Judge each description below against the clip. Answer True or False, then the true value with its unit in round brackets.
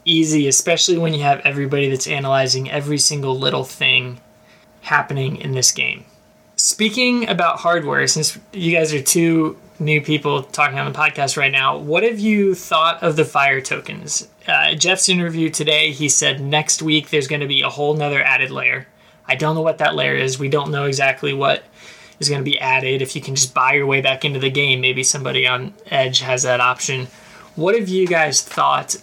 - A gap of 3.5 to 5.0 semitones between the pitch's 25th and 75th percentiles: False (3.1 semitones)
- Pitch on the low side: False (145 Hz)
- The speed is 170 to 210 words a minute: True (200 wpm)